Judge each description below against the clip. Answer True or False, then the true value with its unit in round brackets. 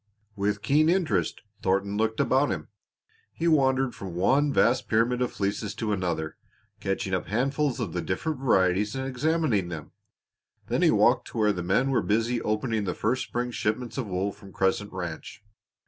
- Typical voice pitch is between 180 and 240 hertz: False (110 Hz)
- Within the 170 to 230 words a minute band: True (175 wpm)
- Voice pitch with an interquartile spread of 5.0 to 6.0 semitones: True (5.3 semitones)